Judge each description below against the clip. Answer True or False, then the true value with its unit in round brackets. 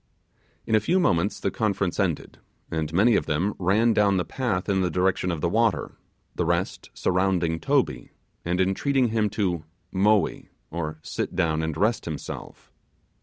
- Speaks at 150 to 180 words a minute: True (165 wpm)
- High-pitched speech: False (95 Hz)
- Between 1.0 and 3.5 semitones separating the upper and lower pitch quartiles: False (3.9 semitones)